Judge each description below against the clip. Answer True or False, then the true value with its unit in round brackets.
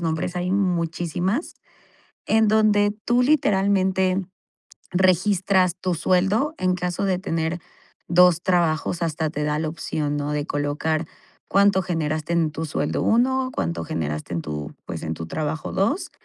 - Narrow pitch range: False (3.7 semitones)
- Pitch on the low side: False (175 Hz)